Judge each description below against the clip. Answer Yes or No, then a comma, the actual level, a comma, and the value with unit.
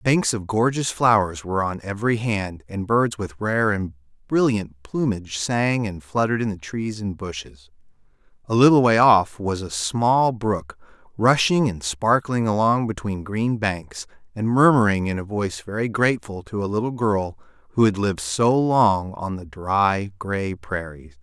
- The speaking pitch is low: Yes, low, 105 Hz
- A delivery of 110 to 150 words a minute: No, average, 165 wpm